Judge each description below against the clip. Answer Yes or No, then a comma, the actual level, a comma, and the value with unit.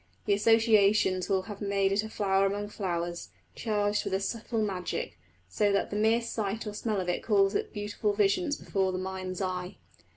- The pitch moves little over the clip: Yes, narrow, 2.0 semitones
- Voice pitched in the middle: No, high, 200 Hz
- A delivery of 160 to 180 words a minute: No, average, 190 wpm